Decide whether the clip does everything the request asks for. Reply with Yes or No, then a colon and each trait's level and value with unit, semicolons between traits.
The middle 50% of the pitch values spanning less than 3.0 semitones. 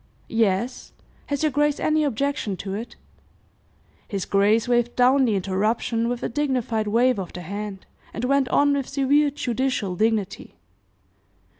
No: average, 5.0 semitones